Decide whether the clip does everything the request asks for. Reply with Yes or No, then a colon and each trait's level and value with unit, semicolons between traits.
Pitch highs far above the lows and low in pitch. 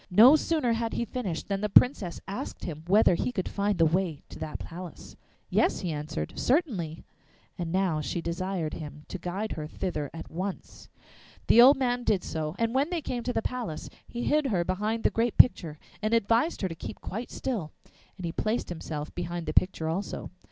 No: wide, 5.9 semitones; high, 190 Hz